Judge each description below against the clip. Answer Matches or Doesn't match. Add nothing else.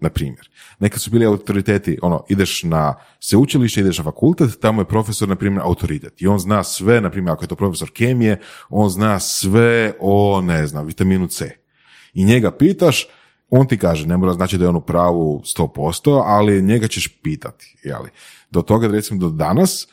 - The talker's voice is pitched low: Matches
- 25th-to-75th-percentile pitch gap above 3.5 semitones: Matches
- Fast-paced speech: Matches